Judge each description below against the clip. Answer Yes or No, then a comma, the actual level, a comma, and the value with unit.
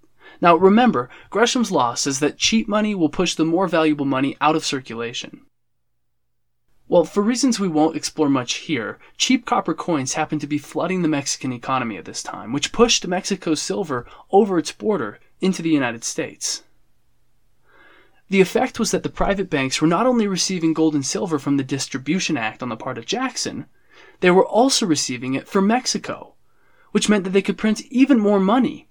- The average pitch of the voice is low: No, medium, 170 Hz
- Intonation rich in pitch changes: Yes, wide, 6.2 semitones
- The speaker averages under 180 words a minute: No, average, 185 wpm